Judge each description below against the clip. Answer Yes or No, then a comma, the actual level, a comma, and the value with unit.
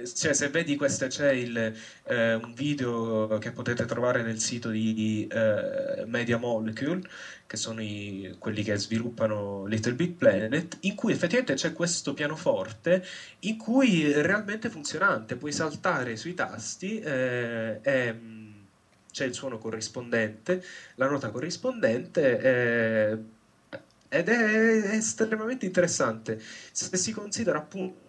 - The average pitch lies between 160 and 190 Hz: No, low, 130 Hz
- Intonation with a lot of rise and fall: Yes, wide, 8.3 semitones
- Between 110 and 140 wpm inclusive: Yes, average, 130 wpm